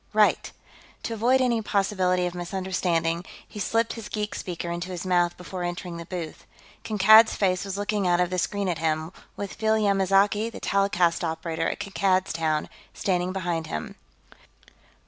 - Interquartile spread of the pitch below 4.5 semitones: Yes, average, 2.9 semitones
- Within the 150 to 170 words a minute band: Yes, average, 165 wpm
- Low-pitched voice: No, medium, 185 Hz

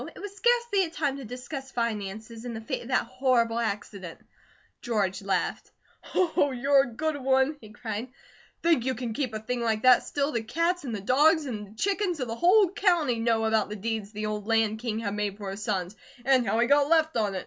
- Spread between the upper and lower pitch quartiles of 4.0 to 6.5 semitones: Yes, average, 4.9 semitones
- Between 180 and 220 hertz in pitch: No, high, 240 Hz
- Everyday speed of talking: No, fast, 225 wpm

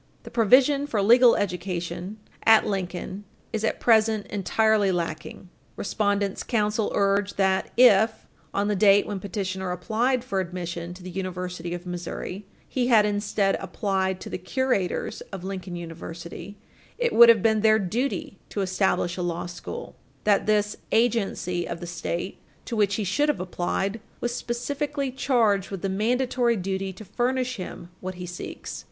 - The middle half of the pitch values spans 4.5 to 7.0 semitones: No, average, 3.5 semitones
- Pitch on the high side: Yes, high, 200 Hz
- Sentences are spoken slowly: No, average, 160 wpm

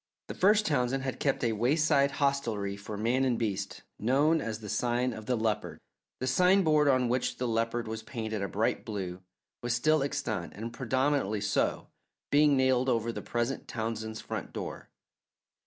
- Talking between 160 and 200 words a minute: Yes, average, 170 wpm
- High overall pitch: No, low, 120 Hz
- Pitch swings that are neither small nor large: Yes, average, 3.8 semitones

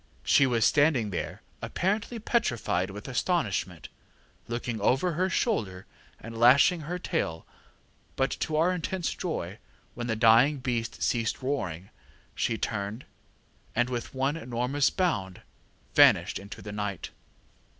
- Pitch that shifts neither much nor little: No, wide, 6.8 semitones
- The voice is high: No, low, 120 Hz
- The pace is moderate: No, slow, 130 wpm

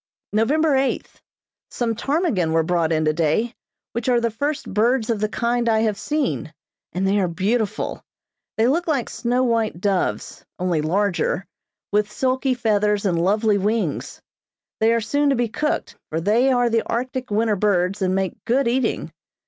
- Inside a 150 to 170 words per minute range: Yes, average, 165 wpm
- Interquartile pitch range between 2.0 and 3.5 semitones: No, average, 4.0 semitones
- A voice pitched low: No, high, 220 Hz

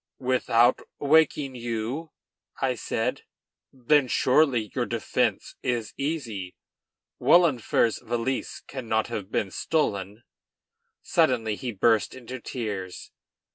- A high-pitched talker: No, low, 120 Hz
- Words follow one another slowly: Yes, slow, 95 wpm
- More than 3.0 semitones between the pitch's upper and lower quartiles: Yes, average, 3.4 semitones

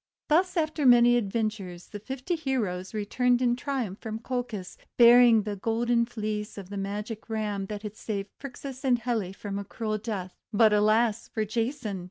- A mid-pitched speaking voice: No, high, 220 Hz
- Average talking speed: Yes, average, 170 wpm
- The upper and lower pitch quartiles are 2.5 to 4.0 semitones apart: Yes, average, 3.0 semitones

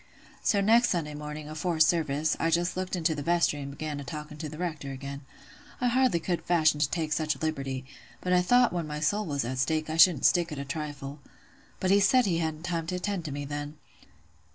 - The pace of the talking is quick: Yes, fast, 225 wpm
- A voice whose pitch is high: No, medium, 155 Hz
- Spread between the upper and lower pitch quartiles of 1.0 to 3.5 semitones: Yes, average, 3.2 semitones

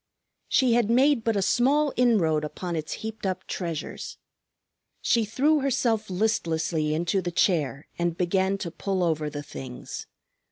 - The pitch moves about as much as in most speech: No, wide, 5.9 semitones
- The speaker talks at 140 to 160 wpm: Yes, average, 150 wpm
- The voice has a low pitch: No, high, 190 Hz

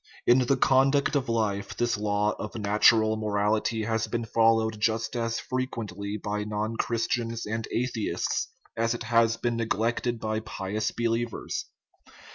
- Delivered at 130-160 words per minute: Yes, average, 150 wpm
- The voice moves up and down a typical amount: No, narrow, 1.7 semitones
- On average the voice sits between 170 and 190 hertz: No, low, 115 Hz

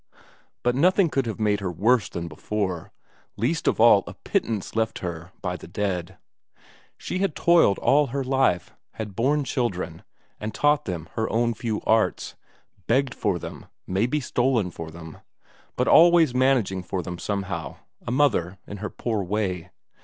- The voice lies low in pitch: Yes, low, 110 Hz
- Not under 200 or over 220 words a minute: No, average, 160 wpm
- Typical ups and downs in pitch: No, wide, 6.2 semitones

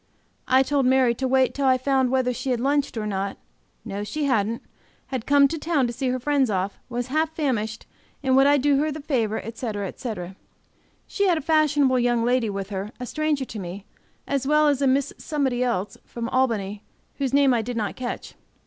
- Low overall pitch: No, very high, 255 Hz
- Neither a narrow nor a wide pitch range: Yes, average, 3.8 semitones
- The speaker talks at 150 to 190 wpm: No, fast, 205 wpm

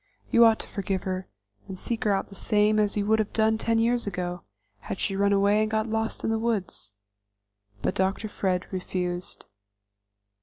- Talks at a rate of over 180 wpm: Yes, average, 190 wpm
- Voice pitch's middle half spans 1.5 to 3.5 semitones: Yes, average, 2.7 semitones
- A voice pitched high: Yes, high, 205 Hz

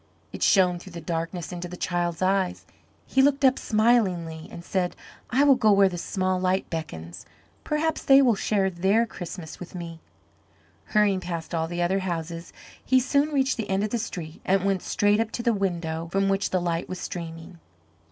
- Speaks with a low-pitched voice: No, medium, 185 Hz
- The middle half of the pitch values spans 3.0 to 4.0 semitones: Yes, average, 3.7 semitones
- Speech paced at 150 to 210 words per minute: Yes, average, 190 wpm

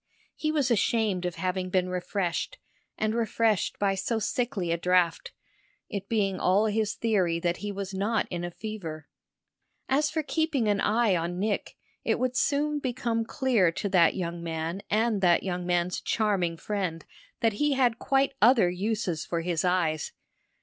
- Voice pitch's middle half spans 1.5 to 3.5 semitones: No, average, 4.5 semitones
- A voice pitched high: Yes, high, 200 Hz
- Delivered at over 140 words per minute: Yes, average, 165 wpm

